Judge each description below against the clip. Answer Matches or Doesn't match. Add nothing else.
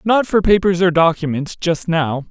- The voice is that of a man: Matches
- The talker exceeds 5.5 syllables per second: Doesn't match